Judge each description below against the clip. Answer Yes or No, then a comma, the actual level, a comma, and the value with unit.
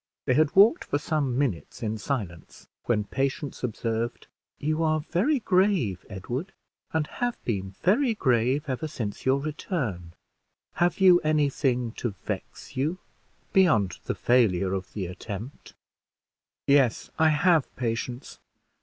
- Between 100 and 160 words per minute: Yes, slow, 135 wpm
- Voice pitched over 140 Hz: No, low, 135 Hz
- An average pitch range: No, wide, 6.0 semitones